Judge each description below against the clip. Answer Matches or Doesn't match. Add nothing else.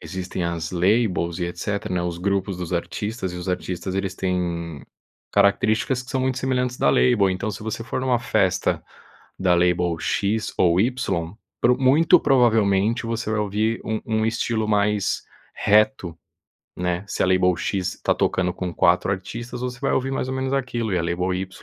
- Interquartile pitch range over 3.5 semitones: Matches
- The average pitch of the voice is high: Doesn't match